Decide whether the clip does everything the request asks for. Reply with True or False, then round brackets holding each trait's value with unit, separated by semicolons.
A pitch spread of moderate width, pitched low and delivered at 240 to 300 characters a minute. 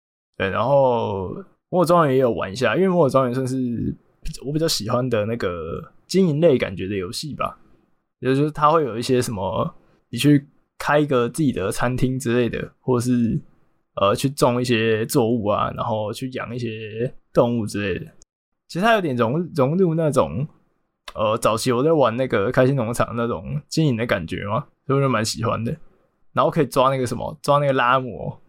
True (4.1 semitones; 130 Hz; 280 characters per minute)